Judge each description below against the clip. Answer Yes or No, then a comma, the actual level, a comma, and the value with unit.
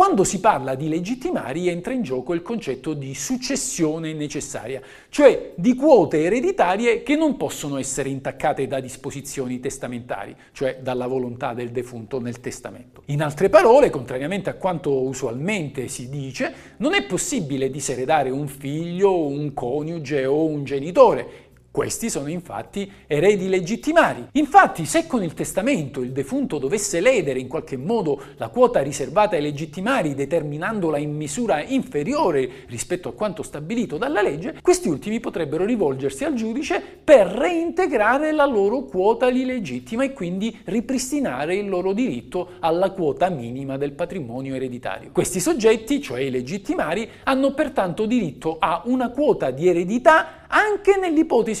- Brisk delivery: No, average, 145 wpm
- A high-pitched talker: No, medium, 175 Hz